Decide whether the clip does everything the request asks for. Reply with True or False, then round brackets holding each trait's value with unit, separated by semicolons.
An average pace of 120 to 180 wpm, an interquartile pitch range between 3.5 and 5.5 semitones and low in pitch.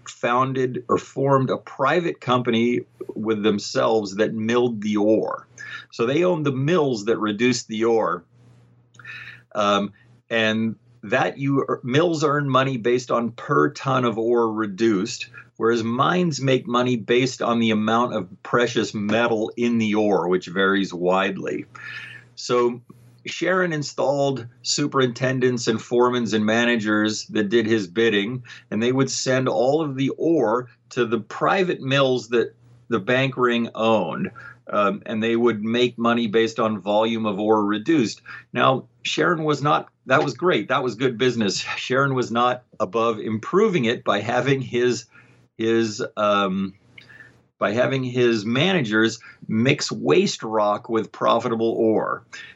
False (145 wpm; 2.6 semitones; 120 Hz)